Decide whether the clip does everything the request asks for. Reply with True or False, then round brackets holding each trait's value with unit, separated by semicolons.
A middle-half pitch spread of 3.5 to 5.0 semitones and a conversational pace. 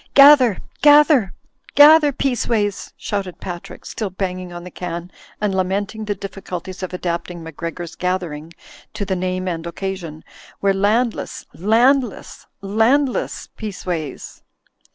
False (3.9 semitones; 125 wpm)